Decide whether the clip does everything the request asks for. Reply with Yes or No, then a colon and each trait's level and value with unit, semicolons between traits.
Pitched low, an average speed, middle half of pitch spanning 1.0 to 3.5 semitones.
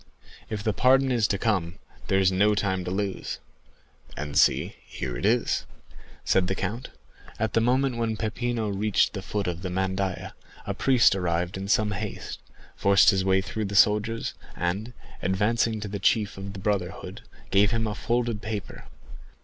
Yes: low, 100 Hz; average, 175 wpm; average, 2.8 semitones